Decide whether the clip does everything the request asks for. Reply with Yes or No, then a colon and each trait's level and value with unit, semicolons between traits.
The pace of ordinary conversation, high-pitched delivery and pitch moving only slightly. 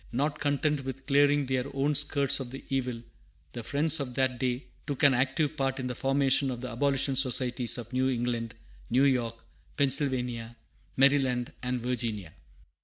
No: average, 165 wpm; low, 130 Hz; narrow, 2.1 semitones